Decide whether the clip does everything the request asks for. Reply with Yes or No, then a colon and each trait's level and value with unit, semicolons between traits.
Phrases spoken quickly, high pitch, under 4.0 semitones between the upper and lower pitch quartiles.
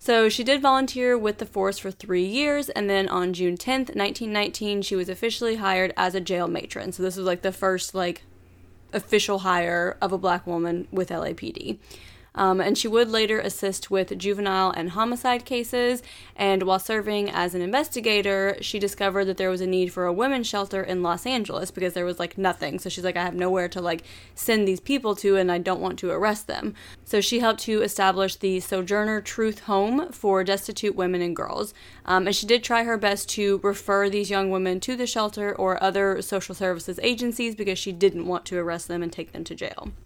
Yes: fast, 210 wpm; high, 195 Hz; average, 2.8 semitones